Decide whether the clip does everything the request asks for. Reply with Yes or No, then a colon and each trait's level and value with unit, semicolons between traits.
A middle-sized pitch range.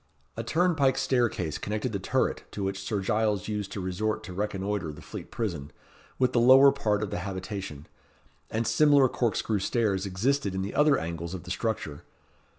Yes: average, 4.0 semitones